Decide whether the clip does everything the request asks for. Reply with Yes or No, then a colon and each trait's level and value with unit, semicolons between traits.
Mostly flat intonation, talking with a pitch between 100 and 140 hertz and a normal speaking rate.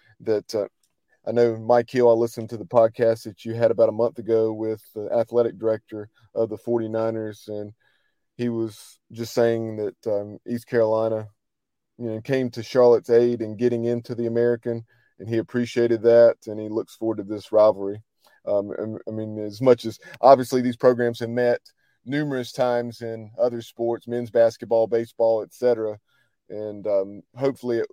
Yes: narrow, 1.5 semitones; low, 115 Hz; average, 175 wpm